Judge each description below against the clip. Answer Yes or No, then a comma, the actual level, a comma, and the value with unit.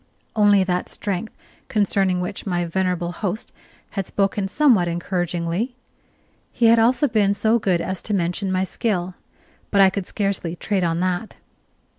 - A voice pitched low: No, high, 190 Hz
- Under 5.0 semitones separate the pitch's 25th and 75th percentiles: Yes, average, 2.8 semitones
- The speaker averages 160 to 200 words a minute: No, average, 150 wpm